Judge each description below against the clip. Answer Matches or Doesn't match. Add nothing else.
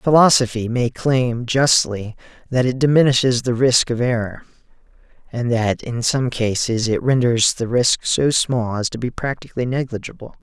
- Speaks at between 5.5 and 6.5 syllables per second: Doesn't match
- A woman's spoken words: Doesn't match